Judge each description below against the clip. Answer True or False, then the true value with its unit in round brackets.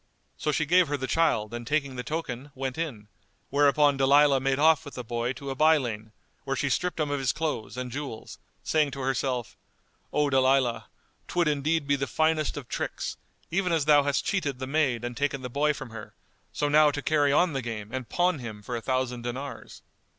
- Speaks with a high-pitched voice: False (140 Hz)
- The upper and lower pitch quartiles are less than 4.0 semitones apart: True (3.3 semitones)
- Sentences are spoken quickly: True (210 wpm)